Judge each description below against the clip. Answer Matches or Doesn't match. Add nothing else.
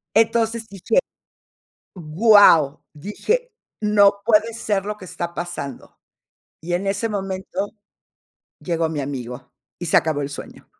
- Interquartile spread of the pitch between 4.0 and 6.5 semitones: Matches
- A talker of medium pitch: Doesn't match